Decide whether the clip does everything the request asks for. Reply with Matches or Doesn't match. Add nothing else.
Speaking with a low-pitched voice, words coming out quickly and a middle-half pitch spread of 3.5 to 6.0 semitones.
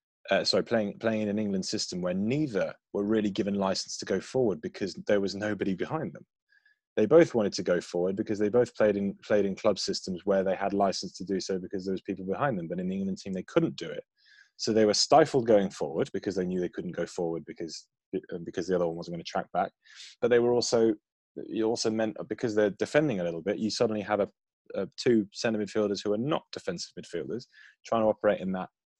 Matches